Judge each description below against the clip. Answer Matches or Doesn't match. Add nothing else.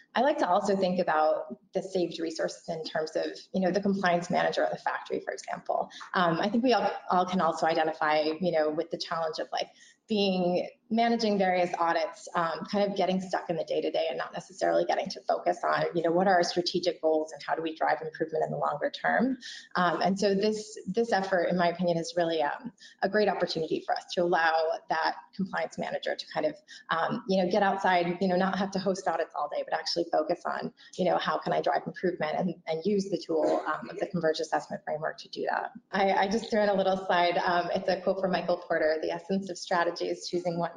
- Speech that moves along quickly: Matches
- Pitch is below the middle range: Doesn't match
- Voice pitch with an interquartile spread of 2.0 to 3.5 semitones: Matches